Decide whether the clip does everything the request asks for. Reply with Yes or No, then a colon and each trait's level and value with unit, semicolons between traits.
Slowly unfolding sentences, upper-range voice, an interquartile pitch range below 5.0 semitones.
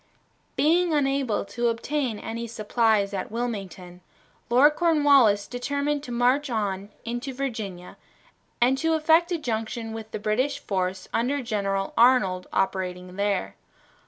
No: slow, 130 wpm; high, 230 Hz; wide, 5.5 semitones